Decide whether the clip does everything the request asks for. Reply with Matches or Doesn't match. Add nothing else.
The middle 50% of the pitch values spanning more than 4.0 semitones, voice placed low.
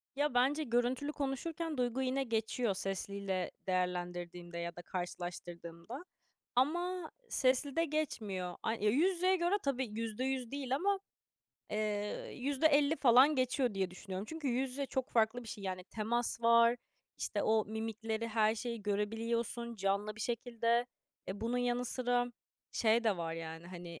Doesn't match